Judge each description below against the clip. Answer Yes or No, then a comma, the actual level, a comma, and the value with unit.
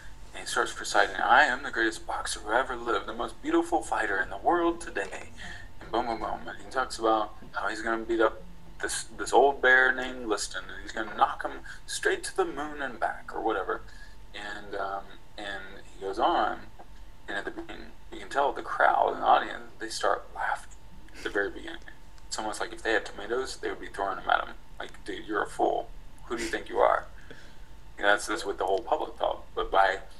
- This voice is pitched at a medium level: No, low, 110 Hz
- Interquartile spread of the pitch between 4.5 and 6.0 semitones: Yes, average, 4.9 semitones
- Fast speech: Yes, fast, 225 wpm